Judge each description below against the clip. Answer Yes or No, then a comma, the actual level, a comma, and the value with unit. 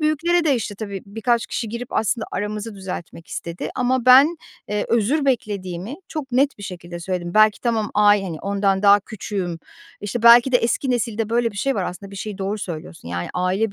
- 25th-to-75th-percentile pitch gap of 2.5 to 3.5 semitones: No, average, 3.9 semitones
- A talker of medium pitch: No, high, 210 Hz